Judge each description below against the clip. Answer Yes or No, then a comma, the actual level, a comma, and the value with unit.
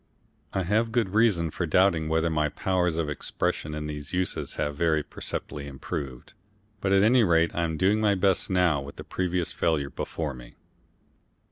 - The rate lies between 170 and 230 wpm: Yes, average, 175 wpm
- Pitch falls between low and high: No, very low, 85 Hz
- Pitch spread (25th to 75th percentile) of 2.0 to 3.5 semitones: No, average, 3.9 semitones